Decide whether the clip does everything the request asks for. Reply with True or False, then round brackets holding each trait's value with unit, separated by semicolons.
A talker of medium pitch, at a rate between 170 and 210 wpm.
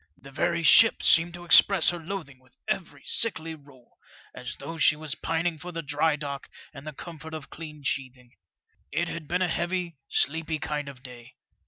True (155 Hz; 185 wpm)